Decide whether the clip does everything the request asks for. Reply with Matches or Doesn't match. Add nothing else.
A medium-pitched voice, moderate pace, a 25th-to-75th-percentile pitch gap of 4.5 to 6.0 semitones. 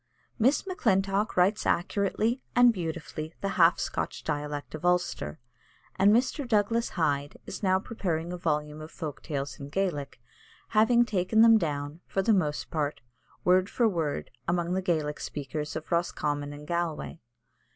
Matches